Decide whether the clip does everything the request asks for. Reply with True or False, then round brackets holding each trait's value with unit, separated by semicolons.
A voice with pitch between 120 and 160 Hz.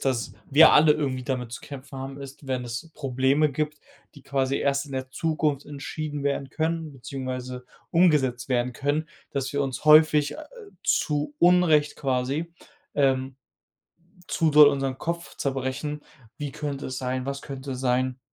True (140 Hz)